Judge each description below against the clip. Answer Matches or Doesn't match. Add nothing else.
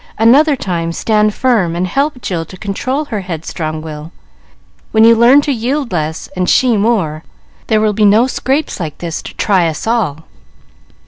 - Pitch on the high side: Matches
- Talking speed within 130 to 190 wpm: Matches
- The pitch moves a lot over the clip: Matches